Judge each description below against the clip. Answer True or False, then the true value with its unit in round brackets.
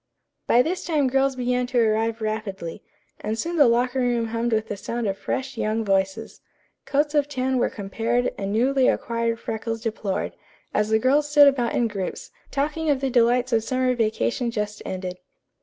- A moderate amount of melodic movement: True (3.2 semitones)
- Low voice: False (235 Hz)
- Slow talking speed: False (185 wpm)